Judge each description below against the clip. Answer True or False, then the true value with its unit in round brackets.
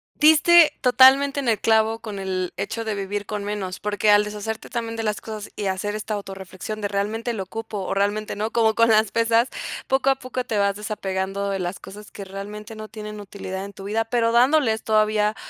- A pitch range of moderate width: False (2.1 semitones)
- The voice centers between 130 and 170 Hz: False (215 Hz)